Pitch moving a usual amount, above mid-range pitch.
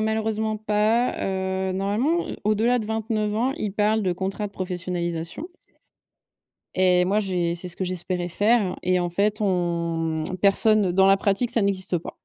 Yes: average, 3.0 semitones; high, 195 Hz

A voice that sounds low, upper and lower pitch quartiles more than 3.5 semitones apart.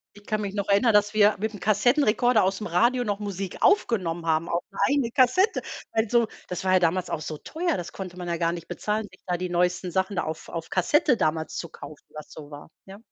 No: high, 195 Hz; average, 4.2 semitones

